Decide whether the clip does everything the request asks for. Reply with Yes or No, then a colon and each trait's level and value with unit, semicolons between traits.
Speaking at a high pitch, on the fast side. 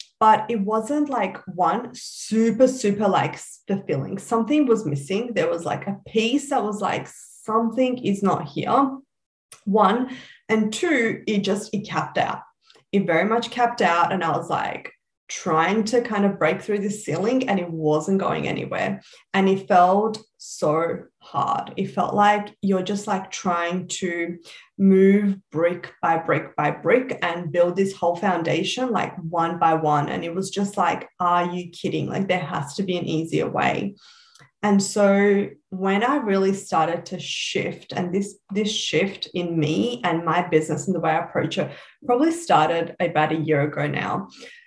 No: high, 195 Hz; average, 170 wpm